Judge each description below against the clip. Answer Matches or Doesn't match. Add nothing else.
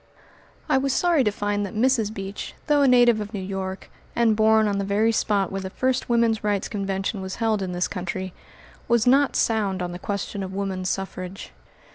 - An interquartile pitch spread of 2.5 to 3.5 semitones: Matches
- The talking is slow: Doesn't match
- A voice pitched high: Matches